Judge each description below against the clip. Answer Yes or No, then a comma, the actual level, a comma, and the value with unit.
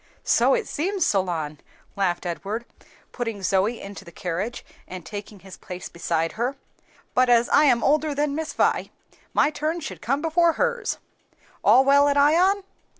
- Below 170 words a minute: Yes, average, 160 wpm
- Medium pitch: No, high, 245 Hz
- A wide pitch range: Yes, wide, 7.9 semitones